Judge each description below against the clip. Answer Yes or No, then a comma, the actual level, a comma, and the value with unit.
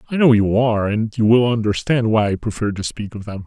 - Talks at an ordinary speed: No, fast, 260 wpm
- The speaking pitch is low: Yes, low, 110 Hz